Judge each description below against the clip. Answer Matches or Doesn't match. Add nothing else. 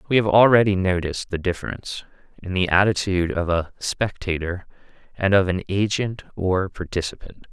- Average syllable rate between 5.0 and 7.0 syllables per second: Matches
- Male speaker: Matches